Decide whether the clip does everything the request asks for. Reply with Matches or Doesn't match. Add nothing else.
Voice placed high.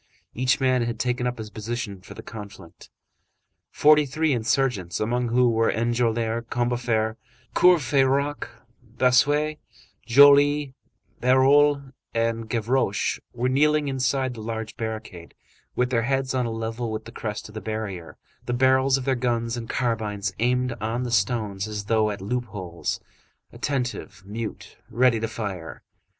Doesn't match